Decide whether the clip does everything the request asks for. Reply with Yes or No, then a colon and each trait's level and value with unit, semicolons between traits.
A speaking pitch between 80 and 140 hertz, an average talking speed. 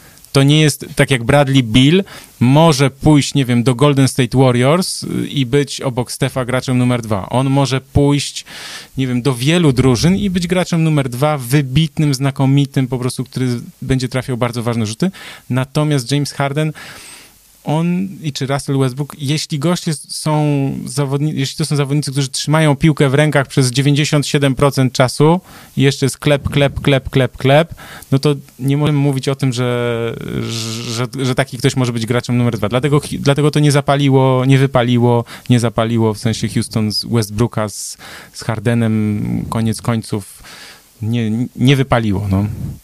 No: low, 135 Hz; fast, 165 wpm